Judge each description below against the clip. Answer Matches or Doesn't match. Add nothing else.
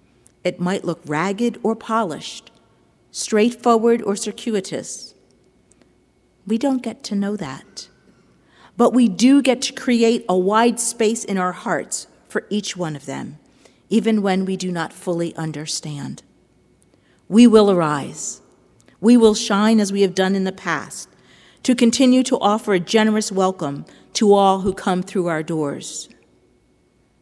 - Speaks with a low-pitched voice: Doesn't match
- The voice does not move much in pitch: Doesn't match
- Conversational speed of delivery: Matches